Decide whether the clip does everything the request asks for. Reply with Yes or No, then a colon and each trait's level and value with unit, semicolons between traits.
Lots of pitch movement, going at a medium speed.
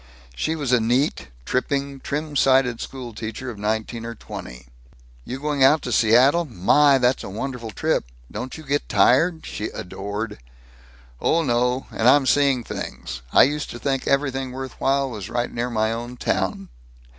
No: average, 3.5 semitones; average, 170 wpm